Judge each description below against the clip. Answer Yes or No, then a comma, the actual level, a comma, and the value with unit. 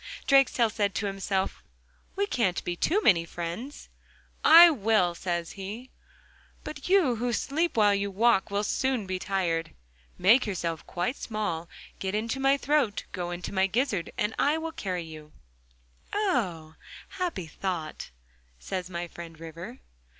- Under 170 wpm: Yes, average, 145 wpm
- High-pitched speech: Yes, high, 200 Hz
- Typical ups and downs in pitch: No, wide, 6.5 semitones